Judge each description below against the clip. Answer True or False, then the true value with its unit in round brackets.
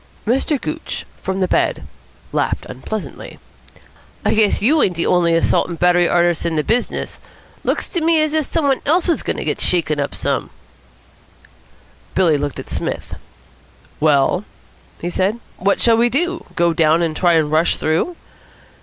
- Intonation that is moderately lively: False (7.1 semitones)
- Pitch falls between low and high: True (180 Hz)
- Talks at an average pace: True (175 wpm)